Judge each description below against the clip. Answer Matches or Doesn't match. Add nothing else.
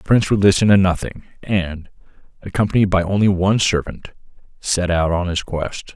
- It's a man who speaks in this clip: Matches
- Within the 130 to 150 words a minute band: Doesn't match